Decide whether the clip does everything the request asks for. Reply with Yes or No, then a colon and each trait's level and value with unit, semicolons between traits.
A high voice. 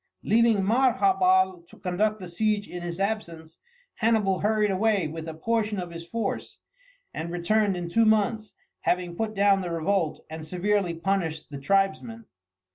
Yes: high, 195 Hz